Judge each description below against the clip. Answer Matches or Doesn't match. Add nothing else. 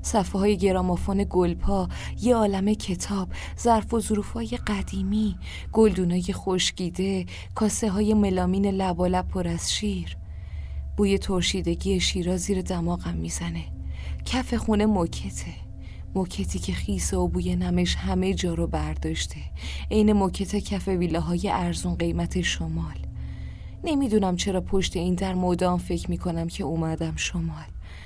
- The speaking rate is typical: Matches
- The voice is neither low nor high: Matches